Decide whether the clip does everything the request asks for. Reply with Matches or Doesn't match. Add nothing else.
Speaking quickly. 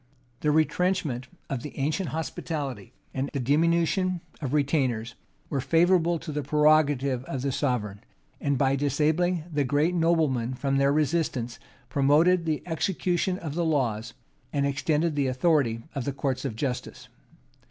Doesn't match